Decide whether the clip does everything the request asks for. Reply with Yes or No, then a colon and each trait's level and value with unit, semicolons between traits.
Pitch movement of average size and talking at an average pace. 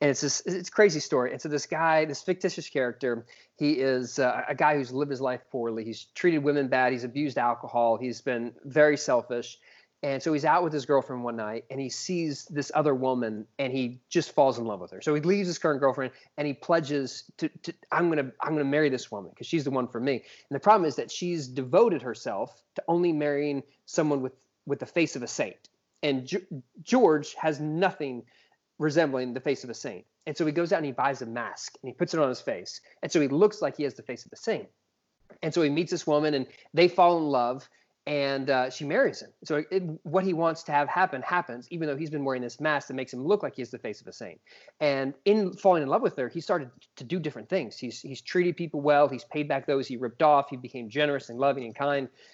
No: average, 4.0 semitones; fast, 250 wpm